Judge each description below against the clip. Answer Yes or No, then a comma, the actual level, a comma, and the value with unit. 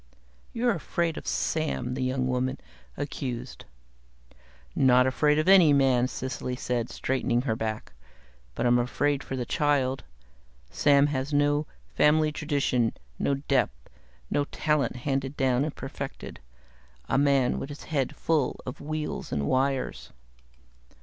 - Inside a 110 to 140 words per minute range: Yes, slow, 135 wpm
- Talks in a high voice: No, low, 135 Hz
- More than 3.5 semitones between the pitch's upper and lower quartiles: No, narrow, 2.5 semitones